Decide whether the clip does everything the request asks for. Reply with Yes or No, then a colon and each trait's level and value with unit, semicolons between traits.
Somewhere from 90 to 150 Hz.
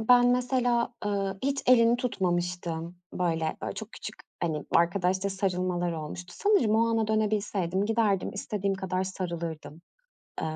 No: high, 195 Hz